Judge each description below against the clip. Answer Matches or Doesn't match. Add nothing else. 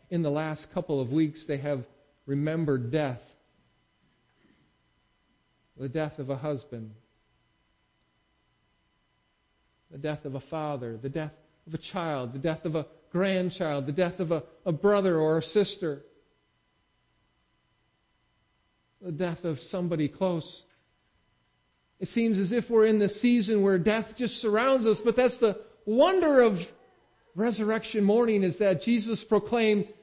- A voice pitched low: Doesn't match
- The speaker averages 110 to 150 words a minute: Matches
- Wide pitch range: Matches